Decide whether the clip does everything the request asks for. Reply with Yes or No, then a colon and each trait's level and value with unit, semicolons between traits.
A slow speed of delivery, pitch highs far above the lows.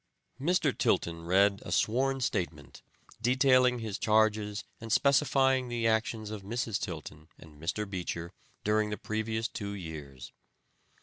No: slow, 130 wpm; average, 4.8 semitones